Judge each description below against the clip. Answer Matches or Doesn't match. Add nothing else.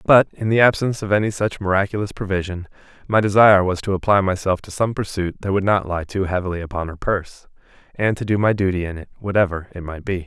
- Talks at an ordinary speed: Doesn't match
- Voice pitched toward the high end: Doesn't match